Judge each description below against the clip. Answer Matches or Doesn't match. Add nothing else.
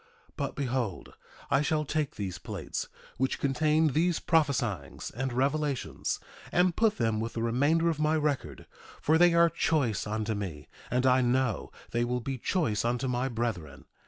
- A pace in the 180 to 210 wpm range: Doesn't match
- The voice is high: Doesn't match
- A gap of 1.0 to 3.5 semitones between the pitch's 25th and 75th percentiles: Doesn't match